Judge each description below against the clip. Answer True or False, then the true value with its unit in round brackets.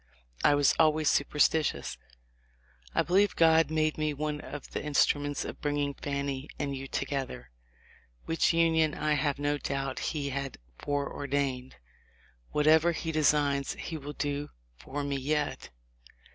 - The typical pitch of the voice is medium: True (145 Hz)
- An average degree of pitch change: False (1.6 semitones)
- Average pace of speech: True (145 wpm)